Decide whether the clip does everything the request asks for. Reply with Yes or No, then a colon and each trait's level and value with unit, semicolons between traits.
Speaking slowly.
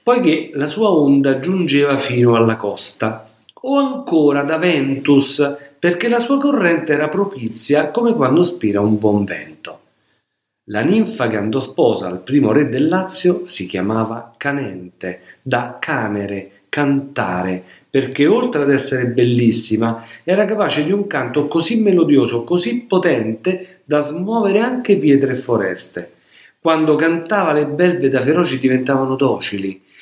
No: average, 135 wpm